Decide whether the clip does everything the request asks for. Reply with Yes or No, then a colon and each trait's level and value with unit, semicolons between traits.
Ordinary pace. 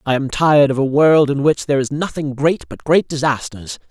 No: fast, 230 wpm